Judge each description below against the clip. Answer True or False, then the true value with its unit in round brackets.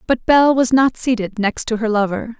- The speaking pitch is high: True (235 Hz)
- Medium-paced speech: False (225 wpm)